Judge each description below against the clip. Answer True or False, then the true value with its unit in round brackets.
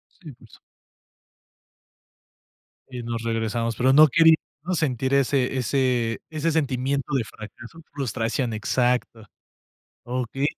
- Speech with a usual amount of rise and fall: True (3.2 semitones)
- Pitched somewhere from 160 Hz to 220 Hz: False (125 Hz)